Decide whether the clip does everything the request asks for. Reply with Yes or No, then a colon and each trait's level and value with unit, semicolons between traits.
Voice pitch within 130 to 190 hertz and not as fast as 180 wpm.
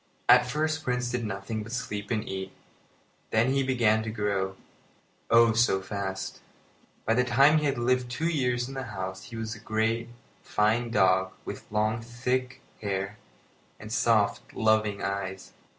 No: low, 115 Hz; average, 160 wpm